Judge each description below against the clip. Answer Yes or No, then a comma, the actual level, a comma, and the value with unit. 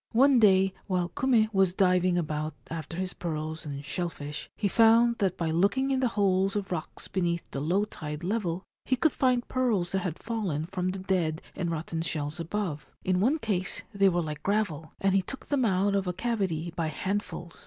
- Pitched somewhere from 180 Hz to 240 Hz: Yes, medium, 185 Hz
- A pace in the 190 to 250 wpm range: Yes, average, 200 wpm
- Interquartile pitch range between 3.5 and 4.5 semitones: Yes, average, 4.0 semitones